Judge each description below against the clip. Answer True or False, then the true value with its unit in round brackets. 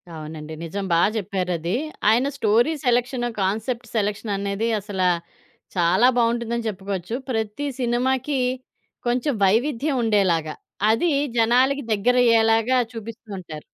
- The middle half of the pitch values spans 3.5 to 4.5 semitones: True (3.9 semitones)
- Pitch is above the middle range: True (225 Hz)